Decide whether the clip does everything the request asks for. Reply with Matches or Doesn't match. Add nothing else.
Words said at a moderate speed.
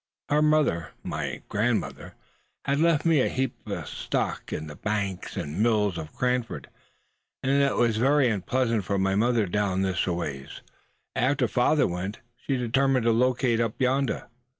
Matches